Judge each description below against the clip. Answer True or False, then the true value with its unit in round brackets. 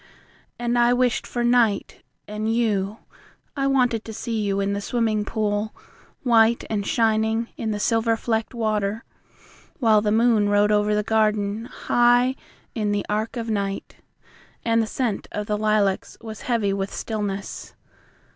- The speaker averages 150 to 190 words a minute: True (155 wpm)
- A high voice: True (220 Hz)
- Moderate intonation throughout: False (2.0 semitones)